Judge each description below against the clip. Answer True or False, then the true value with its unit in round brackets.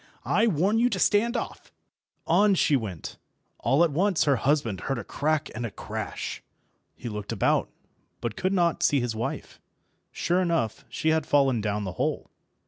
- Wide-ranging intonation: True (7.9 semitones)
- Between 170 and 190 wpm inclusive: True (175 wpm)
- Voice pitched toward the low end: False (145 Hz)